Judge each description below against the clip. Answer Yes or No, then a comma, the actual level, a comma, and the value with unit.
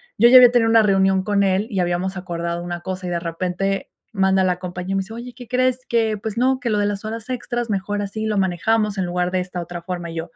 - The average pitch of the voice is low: No, high, 195 Hz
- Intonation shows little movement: No, average, 3.7 semitones